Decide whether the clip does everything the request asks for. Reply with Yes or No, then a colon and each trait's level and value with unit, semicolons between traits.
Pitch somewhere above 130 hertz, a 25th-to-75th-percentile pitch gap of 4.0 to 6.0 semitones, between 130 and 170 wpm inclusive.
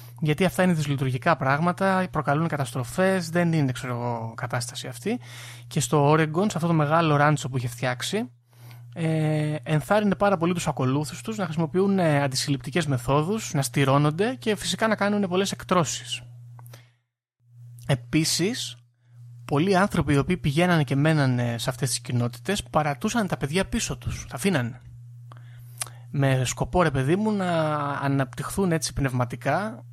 Yes: medium, 140 Hz; wide, 5.6 semitones; average, 140 wpm